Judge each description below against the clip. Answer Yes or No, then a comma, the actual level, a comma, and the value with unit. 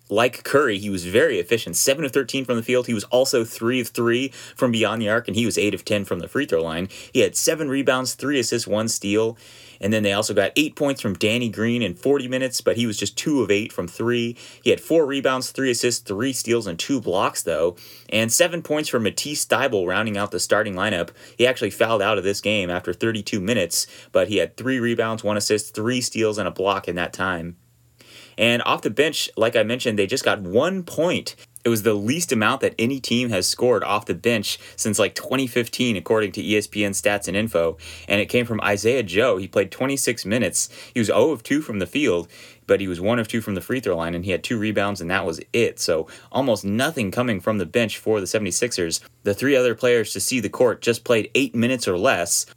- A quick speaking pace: Yes, fast, 235 wpm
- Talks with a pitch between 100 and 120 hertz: Yes, low, 115 Hz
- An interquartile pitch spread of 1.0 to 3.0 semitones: No, average, 3.7 semitones